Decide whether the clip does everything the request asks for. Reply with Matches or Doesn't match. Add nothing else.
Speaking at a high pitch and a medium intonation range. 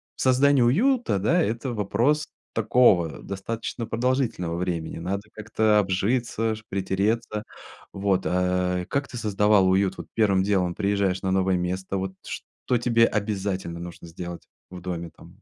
Doesn't match